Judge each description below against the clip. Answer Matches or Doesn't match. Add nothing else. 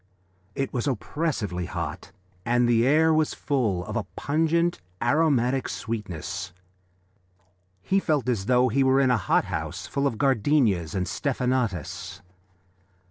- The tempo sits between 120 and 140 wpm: Matches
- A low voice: Matches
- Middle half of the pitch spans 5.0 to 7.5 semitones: Matches